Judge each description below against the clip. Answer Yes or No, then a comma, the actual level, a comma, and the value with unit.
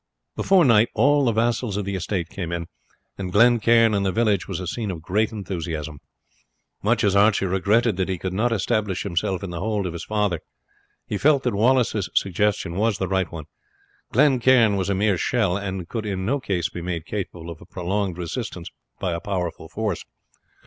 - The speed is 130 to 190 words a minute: No, average, 200 wpm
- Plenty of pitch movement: No, average, 3.7 semitones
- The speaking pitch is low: Yes, low, 100 Hz